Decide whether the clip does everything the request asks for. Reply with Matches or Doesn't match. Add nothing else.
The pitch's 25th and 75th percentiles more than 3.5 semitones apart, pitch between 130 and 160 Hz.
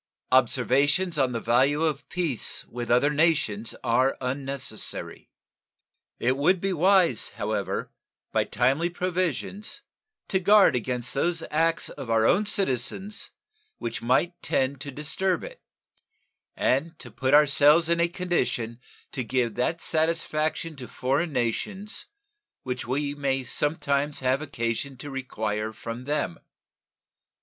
Matches